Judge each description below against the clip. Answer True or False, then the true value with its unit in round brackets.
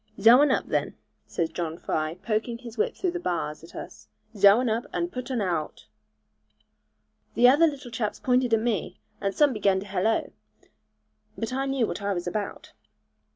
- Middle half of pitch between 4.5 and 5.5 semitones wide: True (5.1 semitones)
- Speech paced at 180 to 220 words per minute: True (185 wpm)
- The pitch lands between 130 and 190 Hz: False (225 Hz)